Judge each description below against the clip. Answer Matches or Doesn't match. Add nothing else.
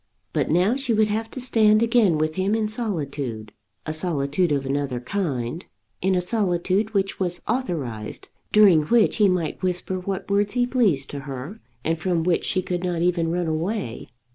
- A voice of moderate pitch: Matches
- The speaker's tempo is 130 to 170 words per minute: Doesn't match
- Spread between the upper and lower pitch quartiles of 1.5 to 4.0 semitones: Doesn't match